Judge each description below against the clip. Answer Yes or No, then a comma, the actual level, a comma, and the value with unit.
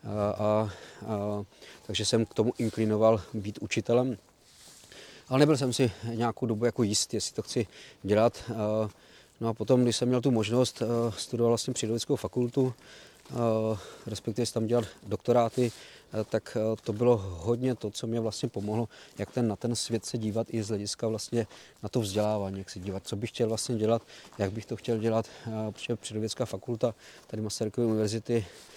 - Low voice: Yes, low, 115 Hz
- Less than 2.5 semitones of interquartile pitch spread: Yes, narrow, 1.9 semitones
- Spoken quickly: Yes, fast, 180 wpm